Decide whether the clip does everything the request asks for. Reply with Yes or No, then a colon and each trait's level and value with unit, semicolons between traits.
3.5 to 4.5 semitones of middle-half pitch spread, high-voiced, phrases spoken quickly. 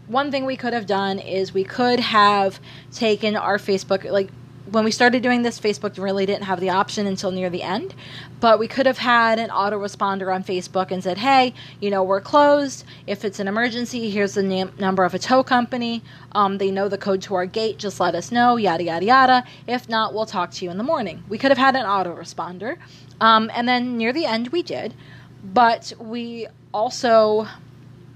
Yes: average, 3.9 semitones; high, 210 Hz; fast, 210 wpm